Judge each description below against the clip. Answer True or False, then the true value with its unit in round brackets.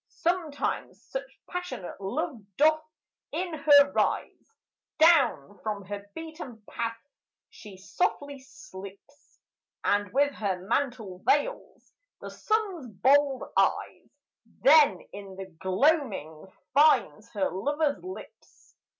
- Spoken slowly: True (105 wpm)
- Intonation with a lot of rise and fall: True (7.5 semitones)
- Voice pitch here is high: True (275 Hz)